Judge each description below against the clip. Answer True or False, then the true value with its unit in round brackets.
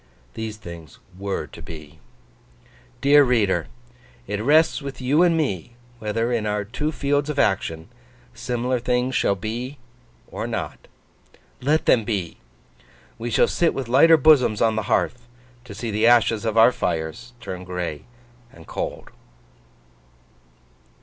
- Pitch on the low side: True (115 Hz)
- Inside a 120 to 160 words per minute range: True (140 wpm)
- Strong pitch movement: False (4.4 semitones)